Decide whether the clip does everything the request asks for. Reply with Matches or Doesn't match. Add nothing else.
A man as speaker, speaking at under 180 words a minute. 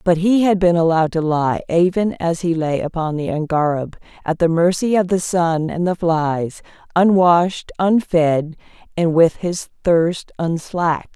Doesn't match